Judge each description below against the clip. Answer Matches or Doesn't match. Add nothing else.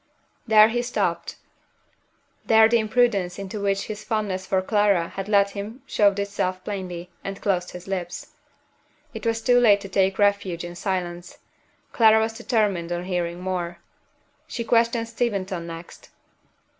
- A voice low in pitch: Doesn't match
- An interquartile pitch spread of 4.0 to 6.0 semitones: Doesn't match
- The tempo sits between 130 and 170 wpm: Matches